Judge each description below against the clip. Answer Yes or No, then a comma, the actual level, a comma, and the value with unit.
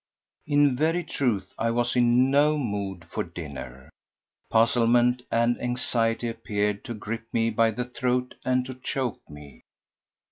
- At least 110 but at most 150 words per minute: Yes, average, 140 wpm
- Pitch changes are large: No, average, 3.3 semitones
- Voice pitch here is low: Yes, low, 120 Hz